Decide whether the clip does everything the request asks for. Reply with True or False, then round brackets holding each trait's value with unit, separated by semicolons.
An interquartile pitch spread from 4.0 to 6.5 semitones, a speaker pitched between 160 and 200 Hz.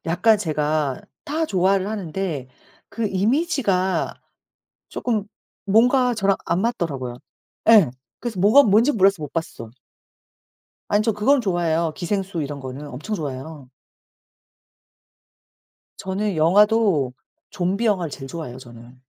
True (6.0 semitones; 185 Hz)